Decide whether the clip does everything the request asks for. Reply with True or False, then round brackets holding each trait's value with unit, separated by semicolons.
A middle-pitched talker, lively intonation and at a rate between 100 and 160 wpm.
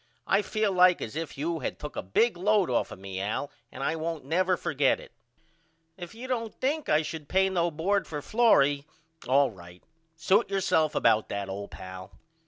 False (160 Hz; 6.2 semitones; 190 wpm)